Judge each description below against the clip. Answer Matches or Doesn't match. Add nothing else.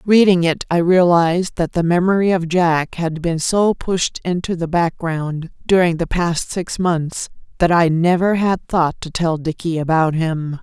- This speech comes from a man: Doesn't match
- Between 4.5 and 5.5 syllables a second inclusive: Doesn't match